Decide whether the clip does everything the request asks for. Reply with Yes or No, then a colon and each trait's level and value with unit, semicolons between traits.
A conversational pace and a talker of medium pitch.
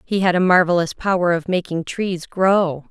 Yes: average, 185 wpm; medium, 180 Hz